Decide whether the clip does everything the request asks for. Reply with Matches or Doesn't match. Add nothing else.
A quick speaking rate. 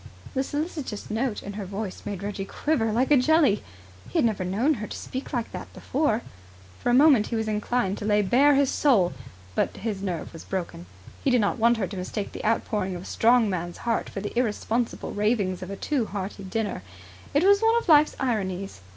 Matches